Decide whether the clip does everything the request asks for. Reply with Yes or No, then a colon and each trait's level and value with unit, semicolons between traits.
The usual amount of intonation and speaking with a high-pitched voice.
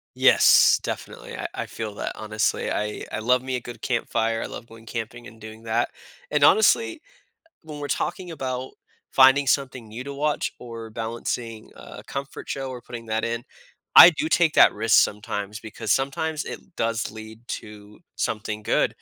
No: average, 3.5 semitones; low, 115 Hz